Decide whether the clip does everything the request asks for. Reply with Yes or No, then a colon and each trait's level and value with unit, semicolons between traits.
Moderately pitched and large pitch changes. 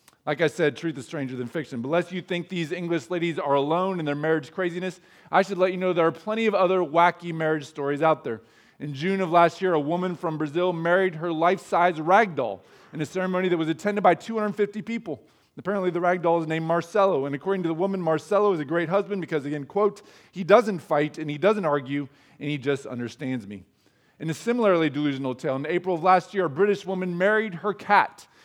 No: medium, 175 Hz; average, 3.7 semitones